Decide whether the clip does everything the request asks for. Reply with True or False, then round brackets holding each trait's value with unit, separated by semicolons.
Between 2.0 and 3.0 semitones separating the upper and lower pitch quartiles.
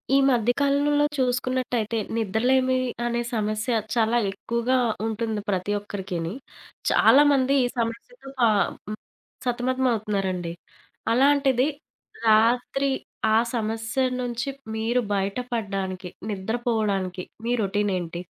False (3.6 semitones)